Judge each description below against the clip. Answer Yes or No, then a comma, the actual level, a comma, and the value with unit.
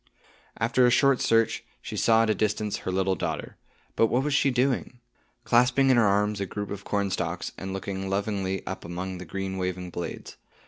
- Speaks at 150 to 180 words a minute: No, average, 190 wpm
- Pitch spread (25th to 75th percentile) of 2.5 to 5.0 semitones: Yes, average, 3.7 semitones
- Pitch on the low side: Yes, low, 100 Hz